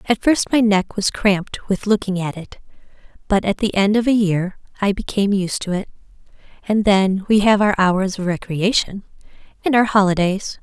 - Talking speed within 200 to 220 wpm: No, average, 185 wpm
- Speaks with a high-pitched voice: Yes, high, 200 Hz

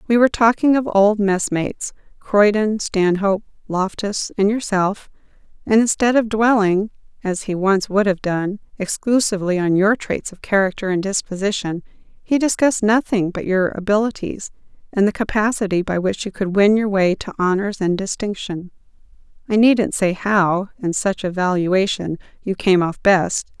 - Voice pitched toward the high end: Yes, high, 200 Hz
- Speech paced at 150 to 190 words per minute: Yes, average, 155 wpm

